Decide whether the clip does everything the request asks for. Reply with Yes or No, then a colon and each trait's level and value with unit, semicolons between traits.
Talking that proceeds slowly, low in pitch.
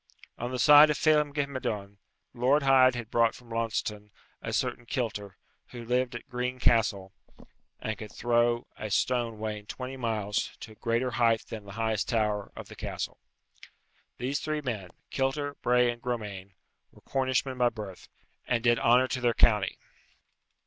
No: average, 165 wpm; low, 120 Hz